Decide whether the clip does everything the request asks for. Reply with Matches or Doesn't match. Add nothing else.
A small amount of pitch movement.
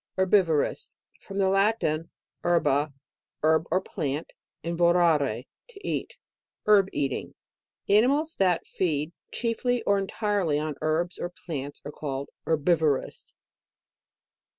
Doesn't match